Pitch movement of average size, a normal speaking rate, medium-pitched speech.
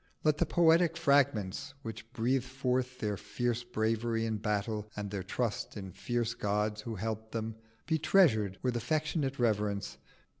No: average, 3.6 semitones; average, 150 wpm; low, 115 Hz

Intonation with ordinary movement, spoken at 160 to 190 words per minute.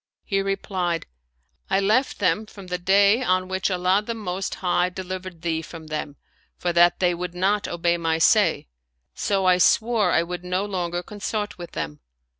No: narrow, 2.3 semitones; average, 180 wpm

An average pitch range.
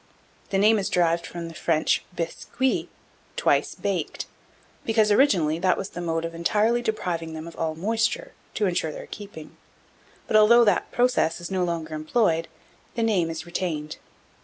Yes: average, 4.7 semitones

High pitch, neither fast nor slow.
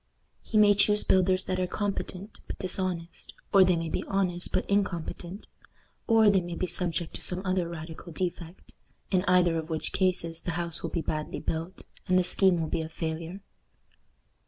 No: medium, 180 Hz; average, 180 wpm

